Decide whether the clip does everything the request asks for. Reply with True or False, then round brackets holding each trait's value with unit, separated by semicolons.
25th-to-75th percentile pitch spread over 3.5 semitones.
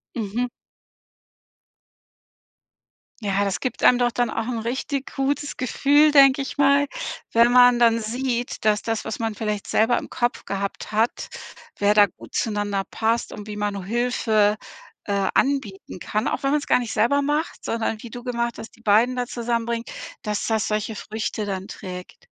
False (2.9 semitones)